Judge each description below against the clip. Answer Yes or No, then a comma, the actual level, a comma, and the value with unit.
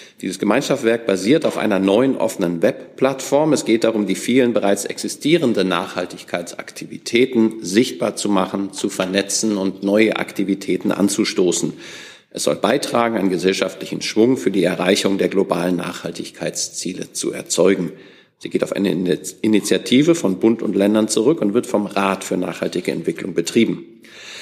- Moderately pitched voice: No, low, 100 Hz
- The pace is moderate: Yes, average, 140 wpm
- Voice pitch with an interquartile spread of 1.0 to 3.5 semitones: Yes, average, 3.1 semitones